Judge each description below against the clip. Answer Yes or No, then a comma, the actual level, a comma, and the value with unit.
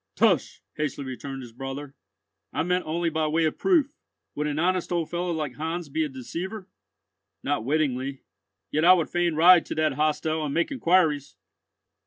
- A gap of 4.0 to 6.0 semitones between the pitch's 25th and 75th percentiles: No, average, 3.3 semitones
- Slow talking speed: No, average, 175 wpm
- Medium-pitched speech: Yes, medium, 155 Hz